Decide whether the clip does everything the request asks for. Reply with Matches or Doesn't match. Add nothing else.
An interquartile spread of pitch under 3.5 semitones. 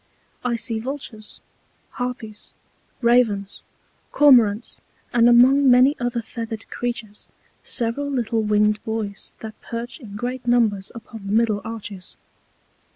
Matches